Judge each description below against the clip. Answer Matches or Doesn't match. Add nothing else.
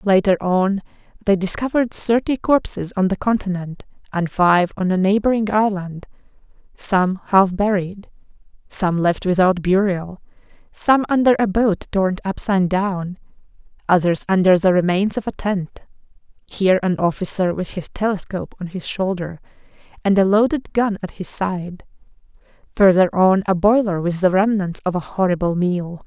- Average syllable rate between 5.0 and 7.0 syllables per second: Doesn't match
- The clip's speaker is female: Matches